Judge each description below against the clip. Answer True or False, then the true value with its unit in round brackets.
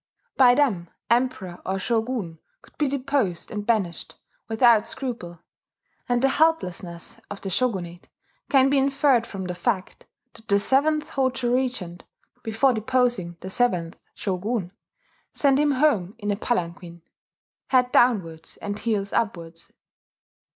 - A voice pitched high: True (225 Hz)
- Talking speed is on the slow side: True (130 wpm)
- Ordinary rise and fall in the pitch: False (5.8 semitones)